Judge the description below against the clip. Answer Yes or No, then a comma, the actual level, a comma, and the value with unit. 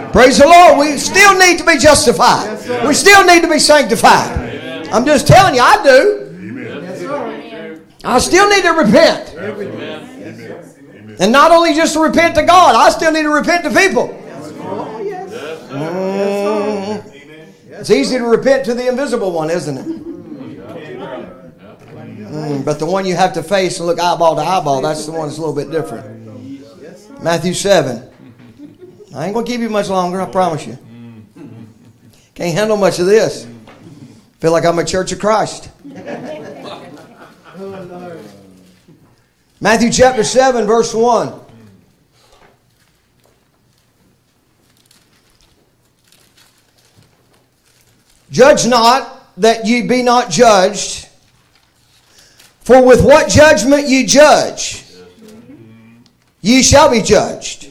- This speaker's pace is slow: Yes, slow, 125 wpm